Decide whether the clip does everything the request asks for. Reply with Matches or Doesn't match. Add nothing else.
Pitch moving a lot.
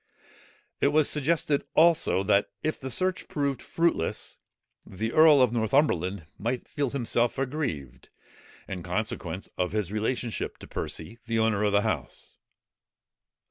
Matches